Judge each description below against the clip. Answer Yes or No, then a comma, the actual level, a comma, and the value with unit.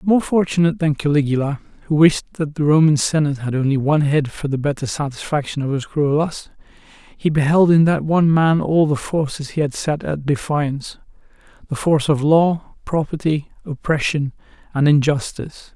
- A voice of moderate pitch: Yes, medium, 150 Hz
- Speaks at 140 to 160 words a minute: No, average, 170 wpm